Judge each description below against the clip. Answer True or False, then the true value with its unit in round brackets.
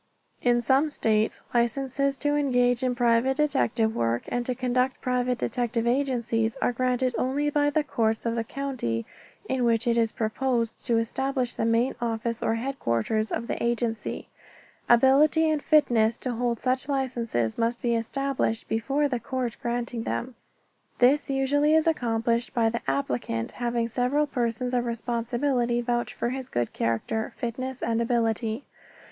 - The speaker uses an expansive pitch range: False (2.5 semitones)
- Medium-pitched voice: False (240 Hz)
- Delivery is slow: False (155 wpm)